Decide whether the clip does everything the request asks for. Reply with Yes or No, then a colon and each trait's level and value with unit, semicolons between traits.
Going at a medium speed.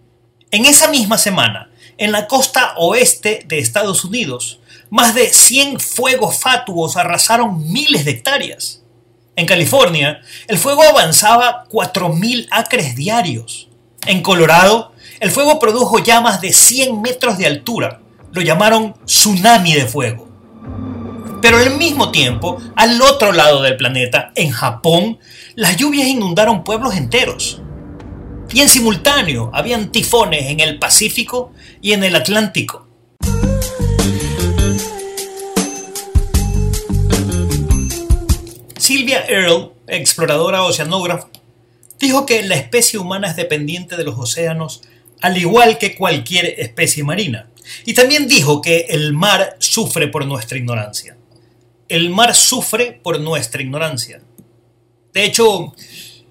No: slow, 115 wpm